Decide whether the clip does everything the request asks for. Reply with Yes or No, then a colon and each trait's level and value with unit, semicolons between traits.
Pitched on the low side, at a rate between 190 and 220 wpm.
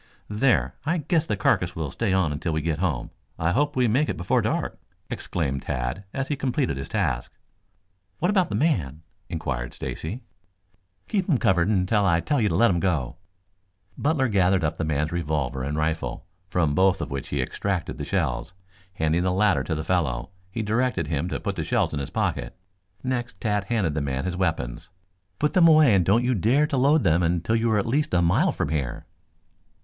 Yes: very low, 90 Hz; average, 200 wpm